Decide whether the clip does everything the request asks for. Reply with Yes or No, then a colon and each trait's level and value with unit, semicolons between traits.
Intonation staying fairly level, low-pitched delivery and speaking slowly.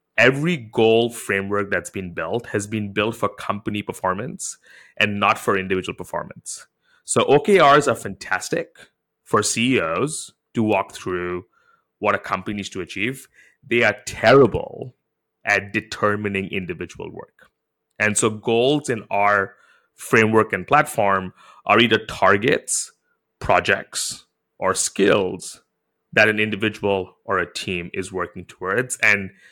Yes: narrow, 2.2 semitones; low, 105 Hz; slow, 130 wpm